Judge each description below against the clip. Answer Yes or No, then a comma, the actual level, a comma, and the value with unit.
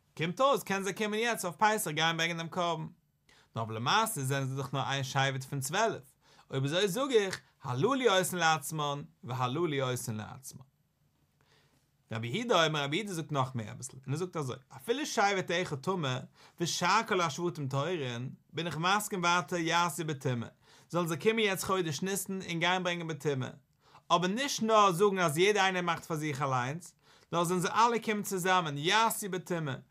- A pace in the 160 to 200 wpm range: Yes, average, 195 wpm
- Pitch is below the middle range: No, medium, 165 Hz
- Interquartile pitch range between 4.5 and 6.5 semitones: Yes, wide, 5.4 semitones